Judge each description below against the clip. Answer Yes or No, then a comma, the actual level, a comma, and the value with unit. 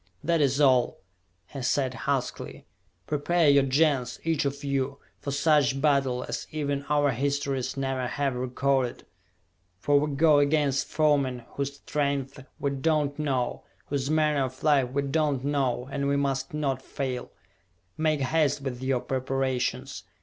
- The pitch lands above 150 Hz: No, medium, 140 Hz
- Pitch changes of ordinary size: No, narrow, 1.7 semitones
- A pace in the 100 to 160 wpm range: Yes, average, 150 wpm